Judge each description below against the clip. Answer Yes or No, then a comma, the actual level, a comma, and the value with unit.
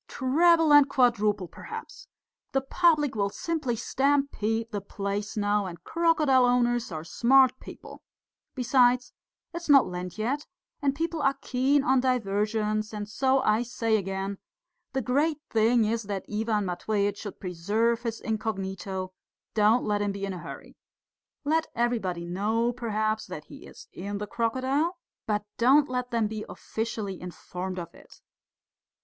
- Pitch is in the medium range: No, high, 225 Hz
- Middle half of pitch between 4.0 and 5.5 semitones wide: Yes, average, 4.3 semitones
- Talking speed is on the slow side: No, average, 145 wpm